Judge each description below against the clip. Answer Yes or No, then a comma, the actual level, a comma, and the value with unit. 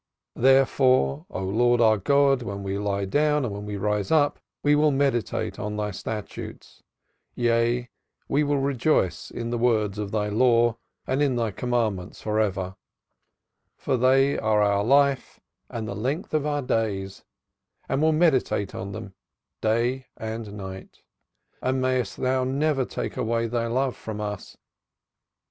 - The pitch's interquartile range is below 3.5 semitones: No, average, 4.3 semitones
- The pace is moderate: Yes, average, 155 wpm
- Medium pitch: No, low, 115 Hz